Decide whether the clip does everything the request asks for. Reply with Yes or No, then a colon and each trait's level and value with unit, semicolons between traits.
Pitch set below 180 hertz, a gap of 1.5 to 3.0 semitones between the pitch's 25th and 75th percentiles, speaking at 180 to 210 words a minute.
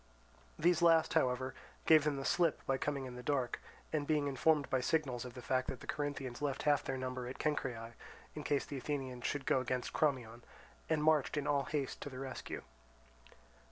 Yes: low, 135 Hz; narrow, 2.6 semitones; average, 190 wpm